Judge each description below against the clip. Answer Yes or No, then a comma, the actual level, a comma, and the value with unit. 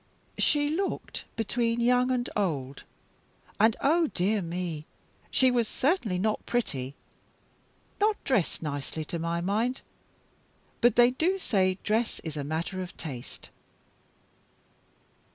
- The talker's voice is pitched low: No, high, 215 Hz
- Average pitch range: No, wide, 6.8 semitones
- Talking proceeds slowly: Yes, slow, 120 wpm